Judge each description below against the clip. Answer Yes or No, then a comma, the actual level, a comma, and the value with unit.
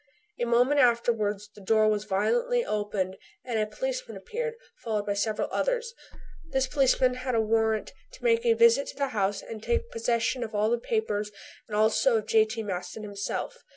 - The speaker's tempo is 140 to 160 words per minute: No, average, 180 wpm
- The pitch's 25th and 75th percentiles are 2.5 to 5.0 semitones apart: No, wide, 5.6 semitones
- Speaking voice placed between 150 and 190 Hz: No, high, 225 Hz